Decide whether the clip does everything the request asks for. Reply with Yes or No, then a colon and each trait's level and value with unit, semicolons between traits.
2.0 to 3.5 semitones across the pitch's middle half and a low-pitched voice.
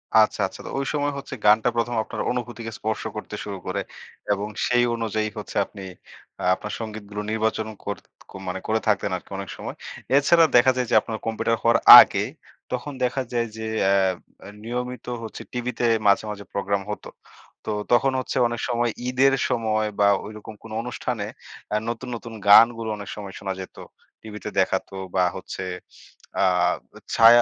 Yes: average, 2.8 semitones; low, 110 Hz